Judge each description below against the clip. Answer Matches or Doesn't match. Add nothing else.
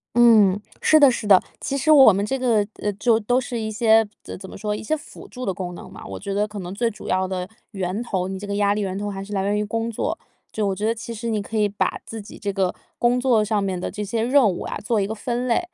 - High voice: Matches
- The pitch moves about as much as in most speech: Matches